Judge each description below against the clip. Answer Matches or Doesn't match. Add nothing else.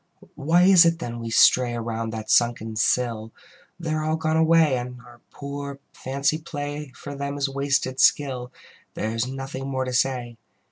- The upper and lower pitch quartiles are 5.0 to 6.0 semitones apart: Doesn't match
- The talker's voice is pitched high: Doesn't match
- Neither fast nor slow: Matches